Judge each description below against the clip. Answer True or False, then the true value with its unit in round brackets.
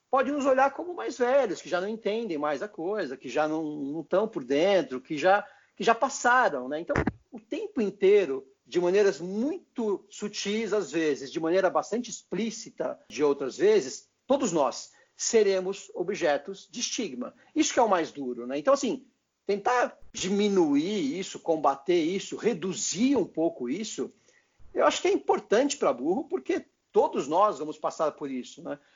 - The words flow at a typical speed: True (170 wpm)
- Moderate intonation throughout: False (7.9 semitones)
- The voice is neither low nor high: False (215 Hz)